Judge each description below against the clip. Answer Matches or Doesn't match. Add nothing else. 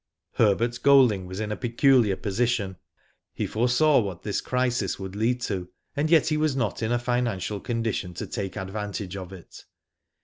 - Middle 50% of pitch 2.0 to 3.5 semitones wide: Doesn't match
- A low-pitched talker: Matches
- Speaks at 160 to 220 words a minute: Matches